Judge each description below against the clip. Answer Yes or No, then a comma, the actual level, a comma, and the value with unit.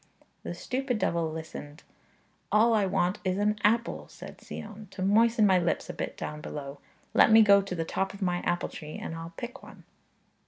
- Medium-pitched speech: No, high, 195 Hz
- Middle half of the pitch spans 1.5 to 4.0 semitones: No, average, 4.6 semitones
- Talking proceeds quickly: No, average, 195 wpm